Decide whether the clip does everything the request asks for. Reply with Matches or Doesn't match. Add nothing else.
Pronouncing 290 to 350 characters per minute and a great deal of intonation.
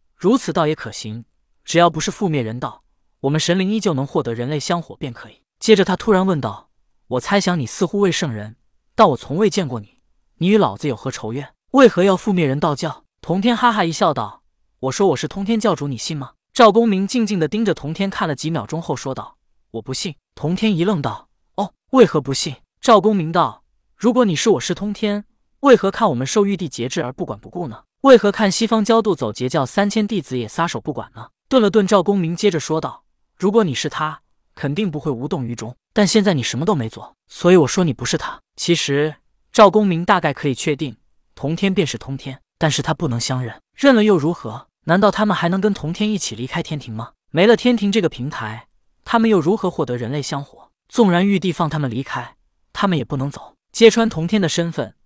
Matches